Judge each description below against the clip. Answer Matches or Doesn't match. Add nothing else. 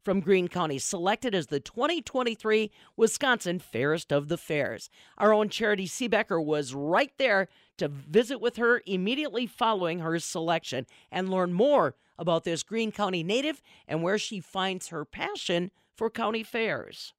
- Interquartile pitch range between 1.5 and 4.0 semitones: Doesn't match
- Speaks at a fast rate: Doesn't match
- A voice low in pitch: Doesn't match